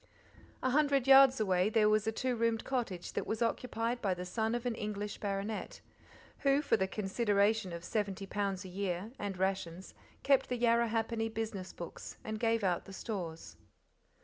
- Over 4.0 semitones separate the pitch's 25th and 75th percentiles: No, average, 3.3 semitones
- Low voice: No, high, 215 Hz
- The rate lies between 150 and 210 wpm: Yes, average, 175 wpm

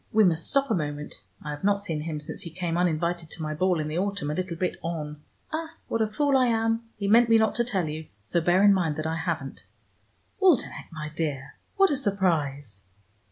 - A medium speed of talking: No, fast, 225 wpm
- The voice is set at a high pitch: No, medium, 175 Hz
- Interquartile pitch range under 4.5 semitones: No, wide, 5.6 semitones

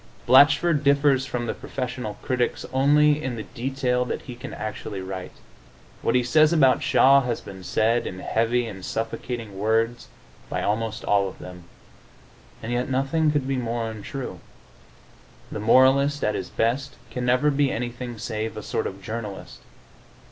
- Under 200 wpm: Yes, average, 160 wpm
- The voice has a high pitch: No, low, 120 Hz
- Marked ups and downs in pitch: No, average, 3.5 semitones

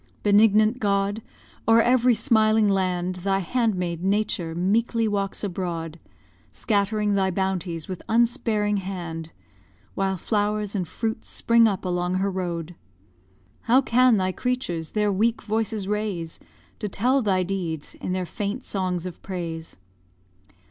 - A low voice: No, high, 200 Hz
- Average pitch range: Yes, average, 3.2 semitones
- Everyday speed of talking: No, slow, 130 wpm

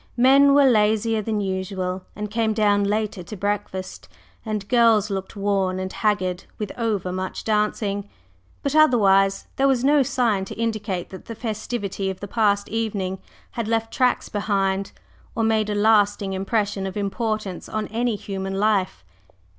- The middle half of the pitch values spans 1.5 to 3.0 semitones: Yes, narrow, 2.5 semitones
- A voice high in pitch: Yes, high, 210 Hz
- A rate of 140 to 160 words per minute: Yes, average, 155 wpm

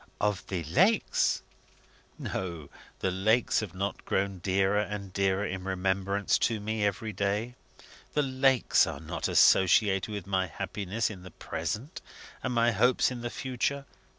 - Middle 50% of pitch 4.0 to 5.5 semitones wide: No, average, 3.5 semitones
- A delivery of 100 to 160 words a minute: Yes, average, 150 wpm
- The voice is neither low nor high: No, low, 100 Hz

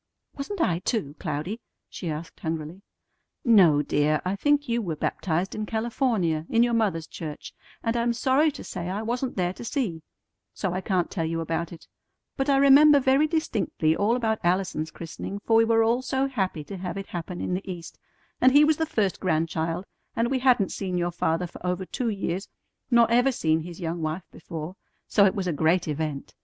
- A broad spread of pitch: Yes, wide, 6.3 semitones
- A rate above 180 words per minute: Yes, average, 200 wpm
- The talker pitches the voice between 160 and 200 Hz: Yes, high, 190 Hz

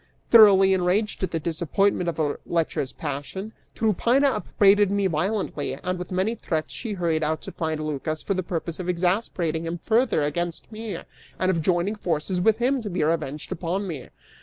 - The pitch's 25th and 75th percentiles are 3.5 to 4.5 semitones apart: Yes, average, 4.1 semitones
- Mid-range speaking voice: Yes, medium, 180 Hz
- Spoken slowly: No, average, 180 wpm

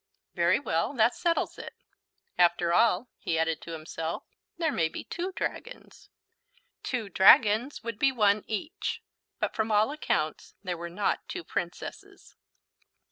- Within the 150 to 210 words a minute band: No, average, 140 wpm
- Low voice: No, high, 205 Hz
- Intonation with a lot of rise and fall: Yes, wide, 6.1 semitones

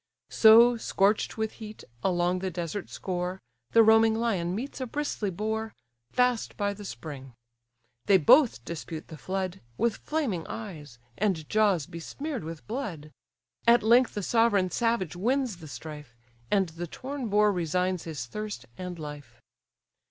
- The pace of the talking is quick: No, average, 145 wpm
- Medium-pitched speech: No, high, 195 Hz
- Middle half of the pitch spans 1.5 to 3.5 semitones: No, average, 4.9 semitones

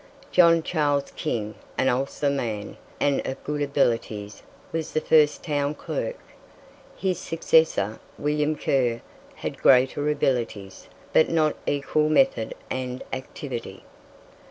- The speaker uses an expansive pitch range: No, average, 3.7 semitones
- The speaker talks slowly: Yes, slow, 115 wpm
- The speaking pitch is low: No, medium, 145 Hz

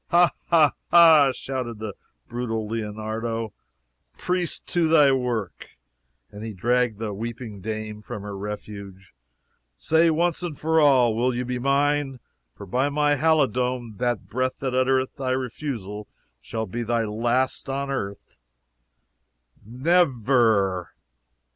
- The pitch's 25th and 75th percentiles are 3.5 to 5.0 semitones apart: Yes, average, 4.2 semitones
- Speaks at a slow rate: Yes, slow, 130 wpm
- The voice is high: No, low, 125 Hz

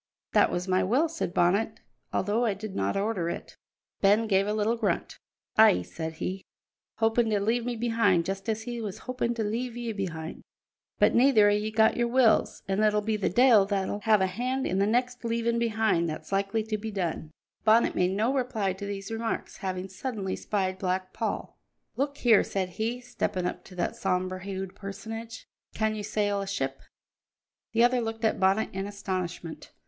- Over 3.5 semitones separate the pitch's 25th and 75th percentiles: No, average, 3.2 semitones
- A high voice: Yes, high, 210 Hz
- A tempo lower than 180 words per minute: No, average, 190 wpm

